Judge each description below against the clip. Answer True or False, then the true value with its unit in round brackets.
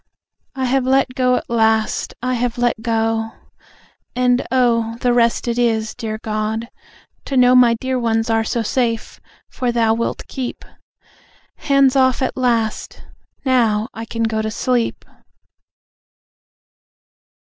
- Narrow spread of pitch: True (2.1 semitones)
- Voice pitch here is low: False (235 Hz)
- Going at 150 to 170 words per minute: False (135 wpm)